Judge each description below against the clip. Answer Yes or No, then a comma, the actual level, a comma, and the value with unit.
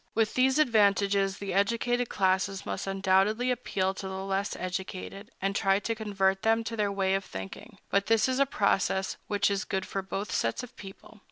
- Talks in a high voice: Yes, high, 200 Hz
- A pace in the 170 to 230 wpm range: Yes, average, 190 wpm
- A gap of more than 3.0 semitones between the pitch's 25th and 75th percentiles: No, narrow, 2.5 semitones